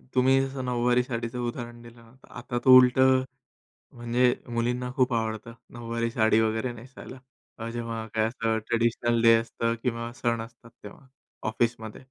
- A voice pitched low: Yes, low, 120 Hz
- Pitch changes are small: Yes, narrow, 1.4 semitones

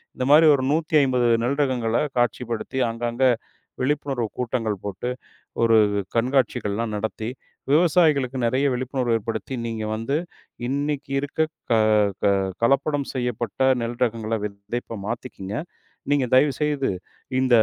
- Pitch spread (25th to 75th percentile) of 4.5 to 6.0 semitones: No, average, 3.3 semitones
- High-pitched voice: No, low, 125 Hz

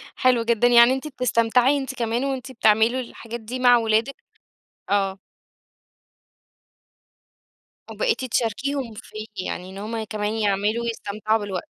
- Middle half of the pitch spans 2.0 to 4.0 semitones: Yes, average, 2.9 semitones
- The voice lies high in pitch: Yes, high, 230 Hz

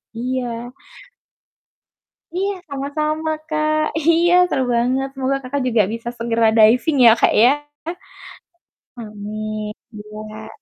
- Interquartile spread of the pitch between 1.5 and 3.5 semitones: No, average, 4.7 semitones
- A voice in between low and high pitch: No, very high, 250 Hz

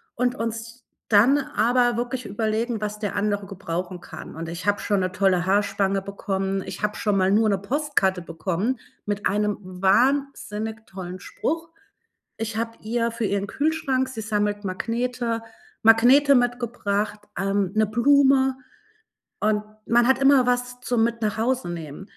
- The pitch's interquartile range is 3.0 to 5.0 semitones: Yes, average, 3.7 semitones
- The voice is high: Yes, high, 215 Hz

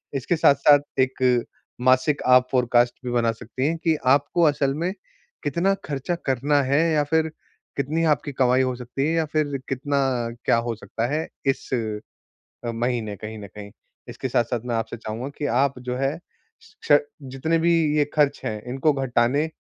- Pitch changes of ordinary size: Yes, average, 3.2 semitones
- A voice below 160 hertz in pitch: Yes, low, 135 Hz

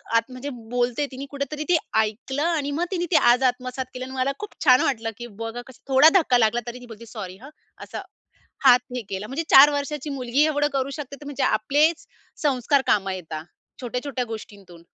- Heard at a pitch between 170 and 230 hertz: No, very high, 255 Hz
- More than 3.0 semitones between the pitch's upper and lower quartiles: Yes, average, 3.6 semitones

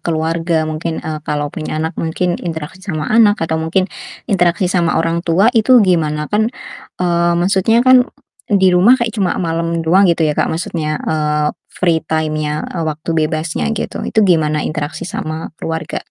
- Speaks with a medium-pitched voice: Yes, medium, 165 Hz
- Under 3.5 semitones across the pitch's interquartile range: Yes, average, 2.8 semitones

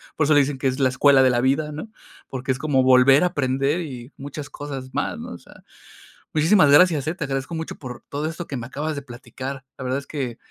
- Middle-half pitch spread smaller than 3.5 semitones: Yes, narrow, 2.6 semitones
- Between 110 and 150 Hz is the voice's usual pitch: Yes, medium, 140 Hz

